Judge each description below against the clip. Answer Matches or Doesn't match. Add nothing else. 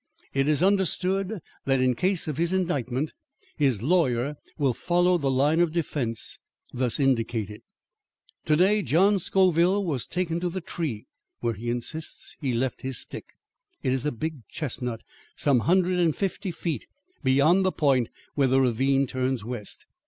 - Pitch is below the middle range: Doesn't match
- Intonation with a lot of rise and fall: Matches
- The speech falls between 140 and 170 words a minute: Matches